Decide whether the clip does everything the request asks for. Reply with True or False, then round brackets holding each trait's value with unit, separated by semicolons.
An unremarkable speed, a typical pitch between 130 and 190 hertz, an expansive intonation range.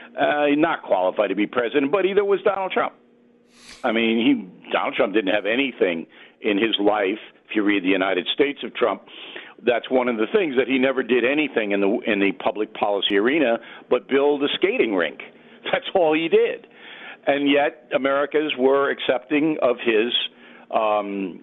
True (180 wpm; 135 Hz; 5.8 semitones)